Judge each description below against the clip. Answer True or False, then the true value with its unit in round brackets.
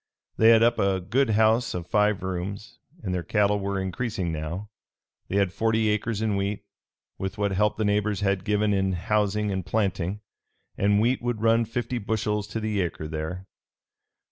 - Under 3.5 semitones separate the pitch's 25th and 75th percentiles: True (2.4 semitones)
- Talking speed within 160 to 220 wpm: True (175 wpm)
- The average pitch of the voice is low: True (105 Hz)